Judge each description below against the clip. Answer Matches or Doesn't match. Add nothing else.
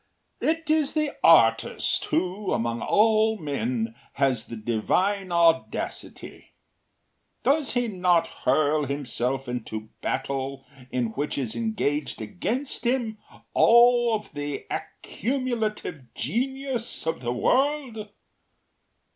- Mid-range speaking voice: Matches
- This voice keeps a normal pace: Doesn't match